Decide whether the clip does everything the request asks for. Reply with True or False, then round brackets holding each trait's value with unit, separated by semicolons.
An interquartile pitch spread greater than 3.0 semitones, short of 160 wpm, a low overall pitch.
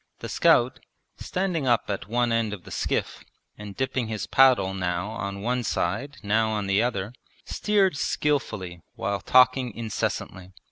True (4.5 semitones; 150 wpm; 110 Hz)